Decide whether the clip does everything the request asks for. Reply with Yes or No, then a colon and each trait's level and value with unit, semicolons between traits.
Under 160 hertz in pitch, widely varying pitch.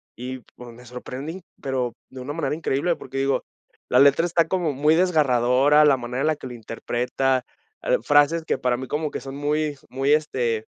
No: low, 135 Hz; average, 3.4 semitones